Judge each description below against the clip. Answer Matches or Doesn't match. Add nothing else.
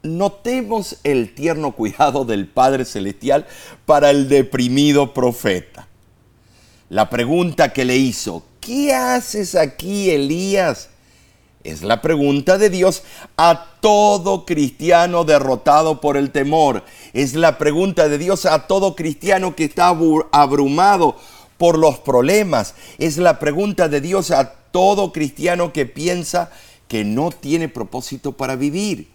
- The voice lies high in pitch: Doesn't match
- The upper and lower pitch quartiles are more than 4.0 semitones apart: Matches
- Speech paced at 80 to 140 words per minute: Matches